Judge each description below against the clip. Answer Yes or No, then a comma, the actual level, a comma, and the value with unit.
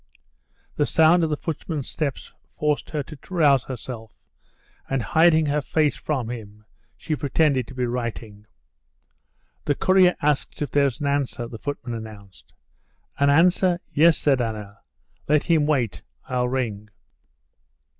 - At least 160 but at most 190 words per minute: No, average, 140 wpm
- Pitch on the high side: No, medium, 140 Hz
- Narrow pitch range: No, average, 4.4 semitones